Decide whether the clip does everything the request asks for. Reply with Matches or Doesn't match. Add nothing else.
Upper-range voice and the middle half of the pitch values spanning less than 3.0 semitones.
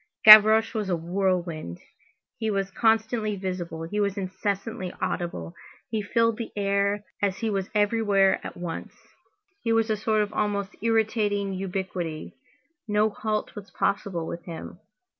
Matches